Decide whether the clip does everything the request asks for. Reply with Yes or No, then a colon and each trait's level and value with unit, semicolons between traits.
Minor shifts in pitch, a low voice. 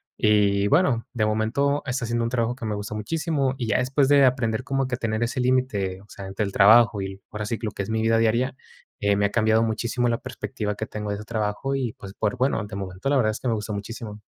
No: average, 3.3 semitones; low, 115 Hz